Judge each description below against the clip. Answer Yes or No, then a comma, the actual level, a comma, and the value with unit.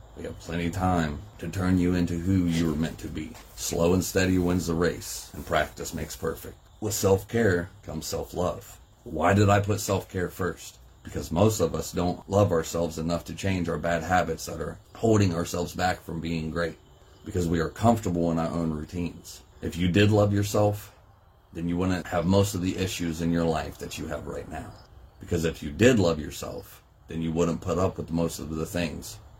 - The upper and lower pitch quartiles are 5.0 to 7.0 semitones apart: No, average, 2.8 semitones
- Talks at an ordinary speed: No, fast, 210 wpm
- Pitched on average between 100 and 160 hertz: No, very low, 90 Hz